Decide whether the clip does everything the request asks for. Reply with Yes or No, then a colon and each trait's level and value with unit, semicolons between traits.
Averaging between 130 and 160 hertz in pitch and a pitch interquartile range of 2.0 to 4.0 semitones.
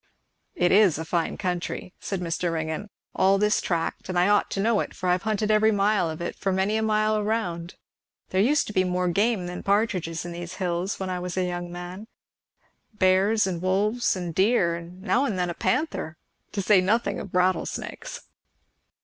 No: medium, 185 Hz; average, 3.1 semitones